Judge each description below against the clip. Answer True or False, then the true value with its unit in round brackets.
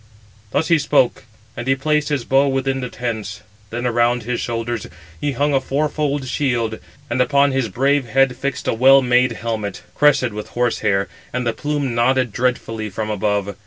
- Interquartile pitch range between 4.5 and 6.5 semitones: False (3.0 semitones)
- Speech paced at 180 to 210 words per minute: True (185 wpm)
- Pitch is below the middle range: True (125 Hz)